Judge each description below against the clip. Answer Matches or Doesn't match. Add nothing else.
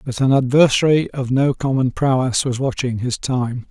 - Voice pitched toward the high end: Doesn't match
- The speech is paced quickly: Doesn't match